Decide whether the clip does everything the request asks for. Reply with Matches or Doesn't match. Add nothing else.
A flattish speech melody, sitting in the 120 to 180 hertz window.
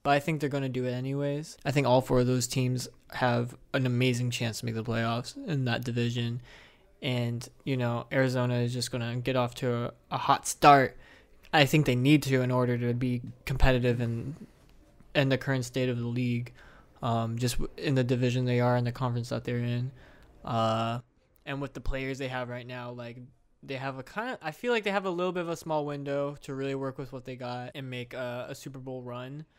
Matches